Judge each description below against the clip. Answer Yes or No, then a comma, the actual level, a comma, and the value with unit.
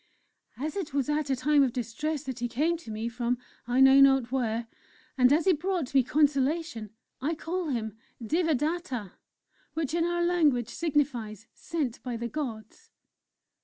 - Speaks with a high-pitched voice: Yes, very high, 275 Hz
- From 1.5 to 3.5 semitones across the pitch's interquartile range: No, average, 4.6 semitones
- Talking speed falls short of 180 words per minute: Yes, average, 165 wpm